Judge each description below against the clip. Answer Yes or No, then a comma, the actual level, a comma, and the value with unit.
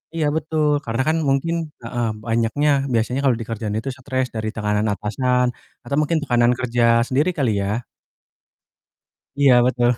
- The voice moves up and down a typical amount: Yes, average, 3.6 semitones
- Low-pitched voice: Yes, low, 125 Hz